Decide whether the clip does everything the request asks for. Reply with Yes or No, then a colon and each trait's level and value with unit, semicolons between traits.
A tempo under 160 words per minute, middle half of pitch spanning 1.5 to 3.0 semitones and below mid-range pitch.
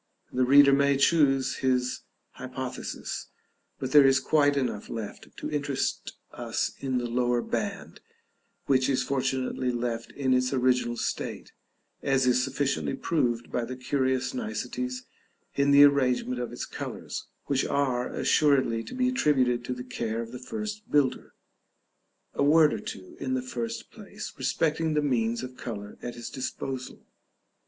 Yes: average, 150 wpm; narrow, 2.4 semitones; low, 130 Hz